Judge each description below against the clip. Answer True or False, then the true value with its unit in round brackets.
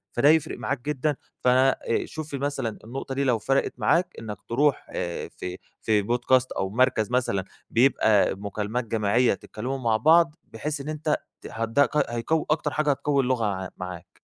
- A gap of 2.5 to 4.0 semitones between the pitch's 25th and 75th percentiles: False (4.6 semitones)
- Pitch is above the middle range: False (125 Hz)